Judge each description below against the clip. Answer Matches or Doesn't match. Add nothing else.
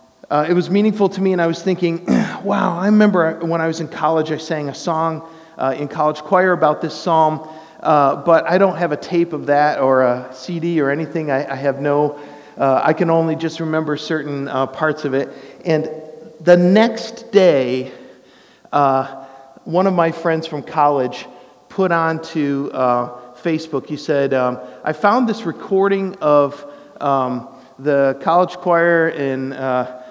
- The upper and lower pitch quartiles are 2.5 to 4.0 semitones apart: Matches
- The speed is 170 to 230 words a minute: Matches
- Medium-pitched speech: Matches